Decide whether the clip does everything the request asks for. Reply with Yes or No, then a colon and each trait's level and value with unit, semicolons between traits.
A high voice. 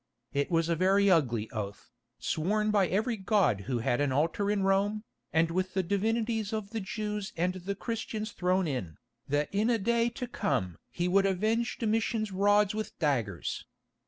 Yes: high, 195 Hz